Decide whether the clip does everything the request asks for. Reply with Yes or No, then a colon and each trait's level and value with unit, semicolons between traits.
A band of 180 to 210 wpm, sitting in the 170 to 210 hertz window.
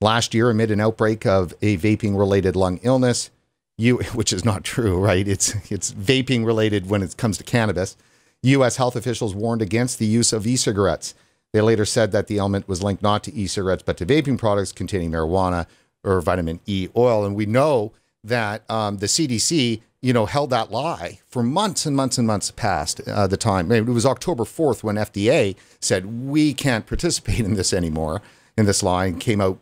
No: average, 195 wpm; low, 110 Hz